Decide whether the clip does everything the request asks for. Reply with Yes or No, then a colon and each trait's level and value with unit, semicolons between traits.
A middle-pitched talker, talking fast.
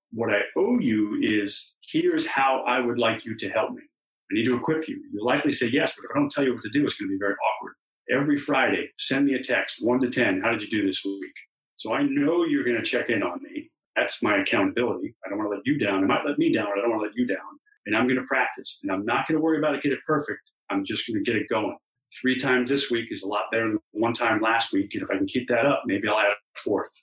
No: low, 130 Hz; fast, 300 wpm